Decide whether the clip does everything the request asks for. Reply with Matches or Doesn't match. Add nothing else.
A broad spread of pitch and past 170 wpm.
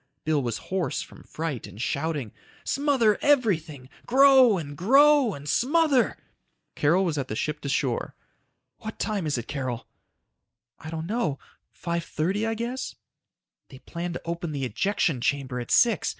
Doesn't match